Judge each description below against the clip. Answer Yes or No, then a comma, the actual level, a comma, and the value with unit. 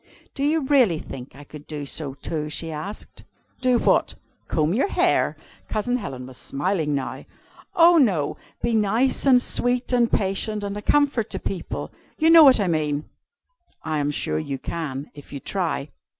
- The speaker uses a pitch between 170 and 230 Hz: Yes, high, 190 Hz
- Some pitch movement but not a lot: No, wide, 8.9 semitones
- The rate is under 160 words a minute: No, average, 175 wpm